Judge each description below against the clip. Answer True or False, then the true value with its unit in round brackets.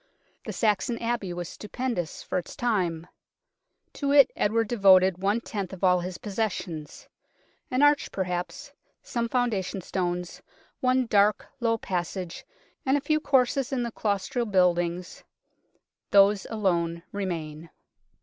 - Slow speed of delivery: True (130 wpm)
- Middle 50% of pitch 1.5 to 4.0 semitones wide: False (5.1 semitones)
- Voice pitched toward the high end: True (200 Hz)